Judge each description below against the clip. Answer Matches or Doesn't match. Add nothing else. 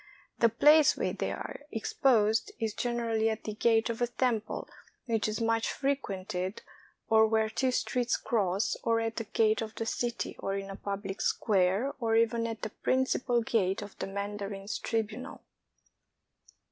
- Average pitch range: Doesn't match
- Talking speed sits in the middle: Matches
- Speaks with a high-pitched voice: Matches